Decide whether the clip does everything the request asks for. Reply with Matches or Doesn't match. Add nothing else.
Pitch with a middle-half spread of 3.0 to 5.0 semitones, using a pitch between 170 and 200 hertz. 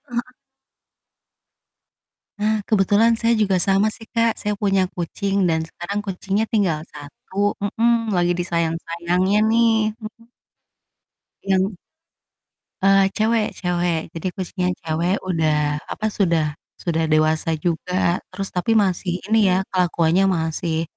Matches